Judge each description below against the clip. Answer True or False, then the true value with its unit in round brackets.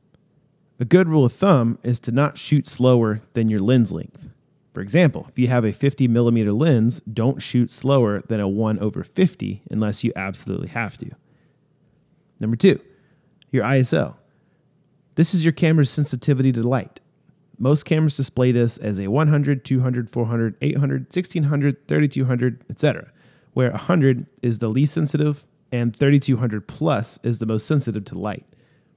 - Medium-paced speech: True (155 wpm)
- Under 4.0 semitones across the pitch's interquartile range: False (4.4 semitones)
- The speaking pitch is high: False (135 Hz)